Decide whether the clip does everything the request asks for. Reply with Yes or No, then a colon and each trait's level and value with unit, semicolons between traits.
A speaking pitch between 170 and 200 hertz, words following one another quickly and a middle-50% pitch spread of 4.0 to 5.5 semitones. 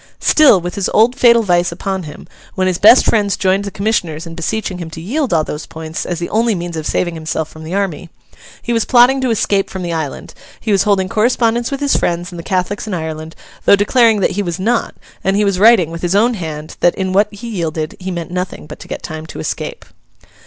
Yes: high, 190 Hz; fast, 240 wpm; average, 4.5 semitones